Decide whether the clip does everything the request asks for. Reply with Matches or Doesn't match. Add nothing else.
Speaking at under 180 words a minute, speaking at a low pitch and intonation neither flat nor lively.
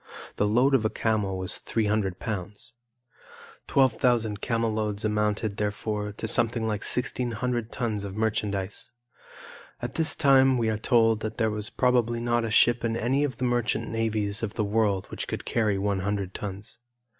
Doesn't match